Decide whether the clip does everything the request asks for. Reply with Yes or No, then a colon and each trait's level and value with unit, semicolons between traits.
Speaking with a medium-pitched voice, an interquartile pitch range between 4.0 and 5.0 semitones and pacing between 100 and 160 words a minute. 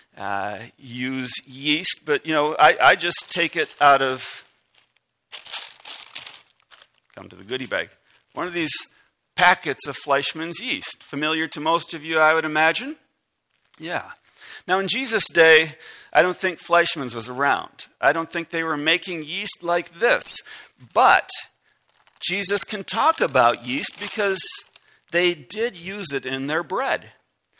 Yes: medium, 165 Hz; average, 4.3 semitones; average, 145 wpm